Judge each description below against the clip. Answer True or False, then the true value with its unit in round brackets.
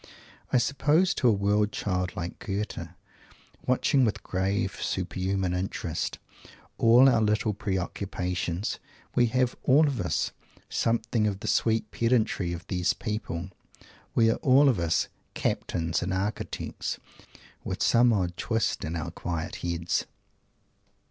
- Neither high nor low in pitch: False (100 Hz)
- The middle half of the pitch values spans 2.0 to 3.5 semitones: False (4.4 semitones)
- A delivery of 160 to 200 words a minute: False (135 wpm)